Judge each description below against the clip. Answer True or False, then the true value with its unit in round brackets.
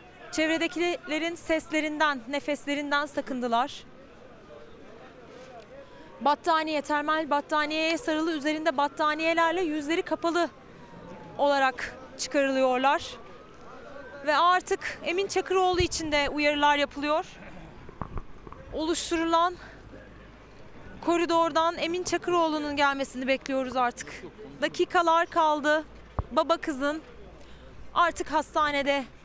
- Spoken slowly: True (70 wpm)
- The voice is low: False (310 Hz)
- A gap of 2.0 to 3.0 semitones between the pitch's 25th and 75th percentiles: True (2.5 semitones)